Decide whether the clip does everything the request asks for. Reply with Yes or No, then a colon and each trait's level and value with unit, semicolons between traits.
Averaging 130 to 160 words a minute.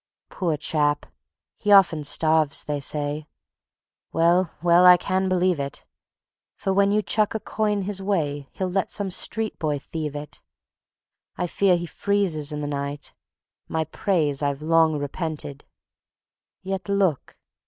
Yes: average, 145 wpm